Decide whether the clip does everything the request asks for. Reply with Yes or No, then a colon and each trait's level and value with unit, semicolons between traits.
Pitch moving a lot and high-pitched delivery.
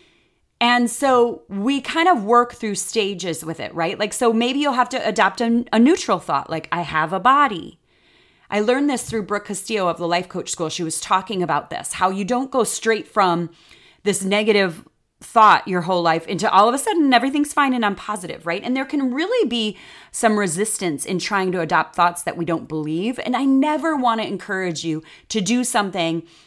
Yes: wide, 5.8 semitones; high, 210 Hz